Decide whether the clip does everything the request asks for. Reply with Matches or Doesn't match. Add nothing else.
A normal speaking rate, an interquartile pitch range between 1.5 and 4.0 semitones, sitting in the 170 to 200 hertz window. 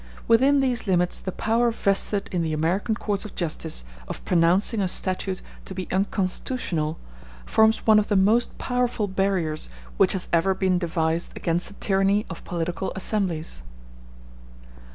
Matches